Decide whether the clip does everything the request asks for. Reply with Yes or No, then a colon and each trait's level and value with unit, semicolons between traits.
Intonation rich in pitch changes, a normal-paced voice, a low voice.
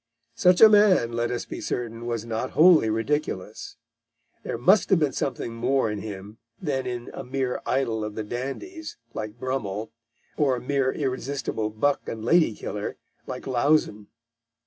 No: average, 4.3 semitones; average, 160 wpm; low, 125 Hz